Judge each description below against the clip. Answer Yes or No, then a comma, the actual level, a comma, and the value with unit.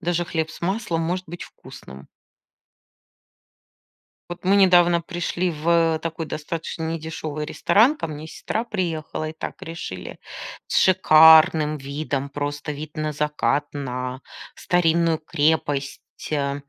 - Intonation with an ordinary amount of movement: No, narrow, 2.3 semitones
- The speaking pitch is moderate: Yes, medium, 160 Hz